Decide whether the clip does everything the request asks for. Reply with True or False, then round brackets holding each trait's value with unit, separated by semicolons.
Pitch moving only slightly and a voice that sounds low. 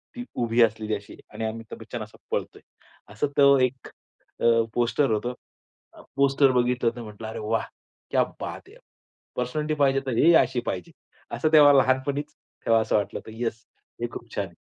False (3.6 semitones; 120 Hz)